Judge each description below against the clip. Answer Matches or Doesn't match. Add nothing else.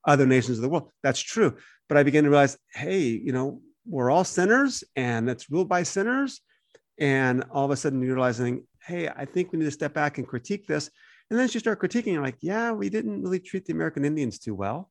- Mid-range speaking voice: Matches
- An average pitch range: Doesn't match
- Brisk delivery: Matches